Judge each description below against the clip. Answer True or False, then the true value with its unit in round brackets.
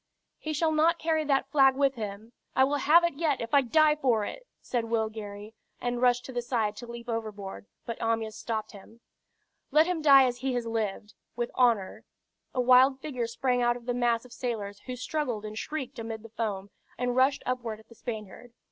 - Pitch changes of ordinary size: True (3.3 semitones)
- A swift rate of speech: True (210 wpm)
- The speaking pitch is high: True (245 Hz)